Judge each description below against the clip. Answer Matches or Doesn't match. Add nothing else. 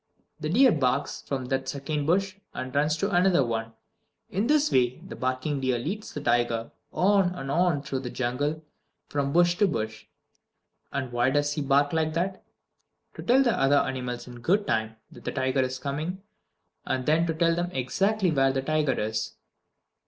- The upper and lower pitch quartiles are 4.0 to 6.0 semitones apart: Matches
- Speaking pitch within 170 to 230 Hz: Doesn't match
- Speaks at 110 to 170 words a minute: Doesn't match